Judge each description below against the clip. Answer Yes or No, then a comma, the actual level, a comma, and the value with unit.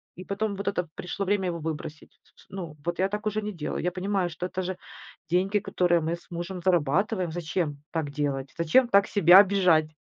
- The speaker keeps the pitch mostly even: No, average, 3.3 semitones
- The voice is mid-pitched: Yes, medium, 180 Hz